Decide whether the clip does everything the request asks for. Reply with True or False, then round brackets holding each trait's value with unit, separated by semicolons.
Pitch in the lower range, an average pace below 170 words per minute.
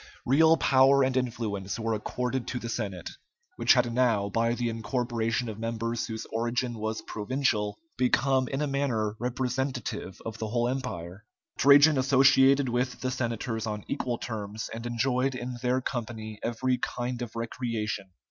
True (120 Hz; 155 wpm)